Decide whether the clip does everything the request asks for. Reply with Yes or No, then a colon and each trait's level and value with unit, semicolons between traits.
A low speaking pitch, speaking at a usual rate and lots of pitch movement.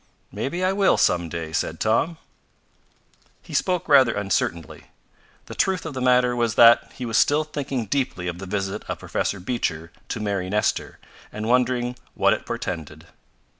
Yes: low, 115 Hz; average, 165 wpm; wide, 5.7 semitones